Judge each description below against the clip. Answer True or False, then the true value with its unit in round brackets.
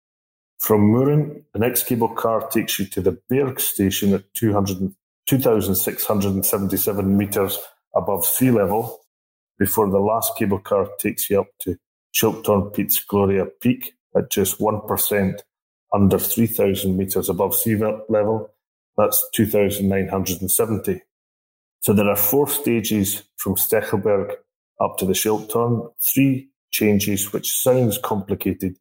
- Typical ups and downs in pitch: True (3.2 semitones)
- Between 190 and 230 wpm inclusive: False (135 wpm)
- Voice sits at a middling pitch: False (105 Hz)